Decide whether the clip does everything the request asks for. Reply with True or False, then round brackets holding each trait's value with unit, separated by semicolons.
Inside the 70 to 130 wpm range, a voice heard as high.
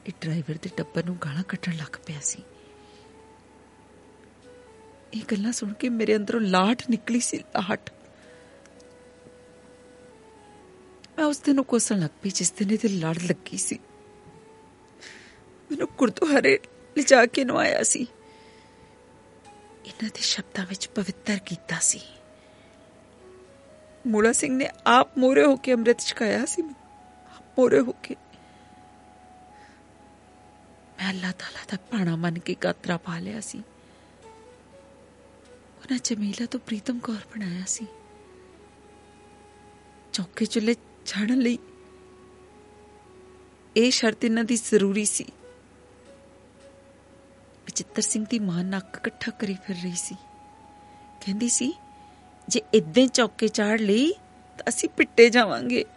True (120 wpm; 215 Hz)